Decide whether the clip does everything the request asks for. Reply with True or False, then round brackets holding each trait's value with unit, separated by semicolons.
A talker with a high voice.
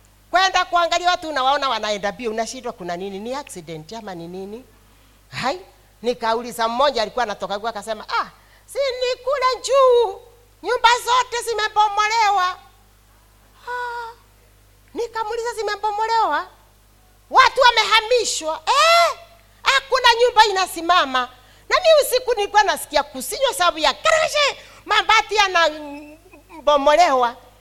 True (345 Hz)